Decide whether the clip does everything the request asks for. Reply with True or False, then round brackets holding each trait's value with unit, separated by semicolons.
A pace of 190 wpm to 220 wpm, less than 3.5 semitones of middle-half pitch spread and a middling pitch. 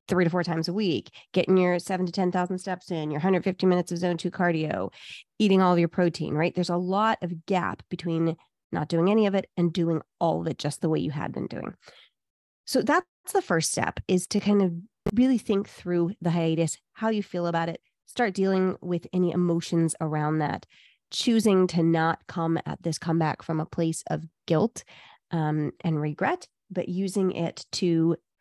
True (200 wpm; 2.4 semitones; 175 Hz)